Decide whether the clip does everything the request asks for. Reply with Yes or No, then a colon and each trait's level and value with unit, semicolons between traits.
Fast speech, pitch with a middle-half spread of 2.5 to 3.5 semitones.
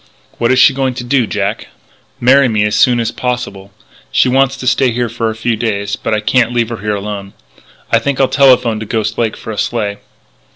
Yes: fast, 220 wpm; average, 2.9 semitones